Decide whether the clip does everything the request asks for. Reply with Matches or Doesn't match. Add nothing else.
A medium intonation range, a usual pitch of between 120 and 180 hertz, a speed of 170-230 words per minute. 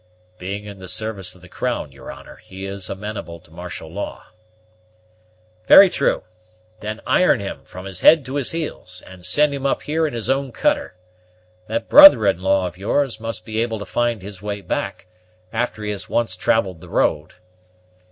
Doesn't match